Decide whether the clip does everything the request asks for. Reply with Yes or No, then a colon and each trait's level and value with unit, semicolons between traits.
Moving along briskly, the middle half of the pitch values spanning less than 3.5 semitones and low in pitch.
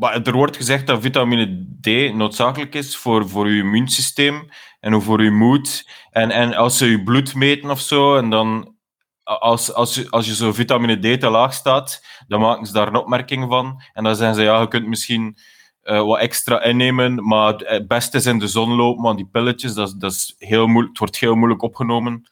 Yes: fast, 210 wpm; narrow, 2.5 semitones; low, 115 Hz